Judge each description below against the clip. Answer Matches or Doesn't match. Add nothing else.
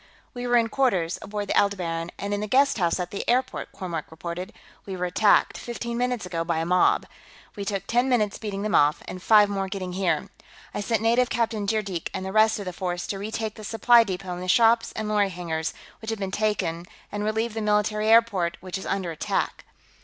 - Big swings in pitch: Doesn't match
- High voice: Matches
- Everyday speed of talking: Doesn't match